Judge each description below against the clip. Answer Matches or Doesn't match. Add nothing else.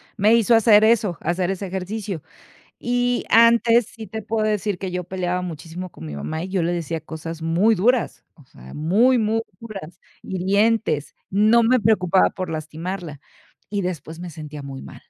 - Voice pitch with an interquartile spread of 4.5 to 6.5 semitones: Matches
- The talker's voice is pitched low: Doesn't match